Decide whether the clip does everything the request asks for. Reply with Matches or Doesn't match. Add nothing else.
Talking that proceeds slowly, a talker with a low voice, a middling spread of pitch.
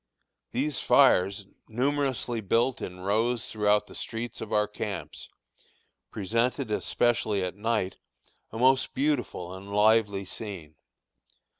Matches